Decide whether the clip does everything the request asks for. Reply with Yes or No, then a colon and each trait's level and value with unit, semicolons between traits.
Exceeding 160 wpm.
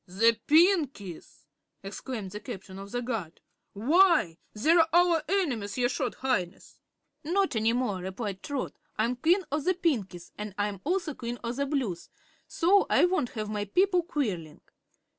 No: average, 155 wpm